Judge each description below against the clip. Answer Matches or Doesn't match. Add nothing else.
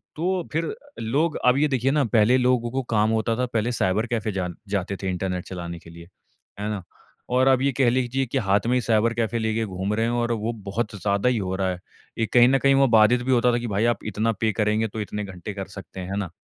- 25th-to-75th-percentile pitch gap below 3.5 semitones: Doesn't match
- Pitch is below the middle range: Matches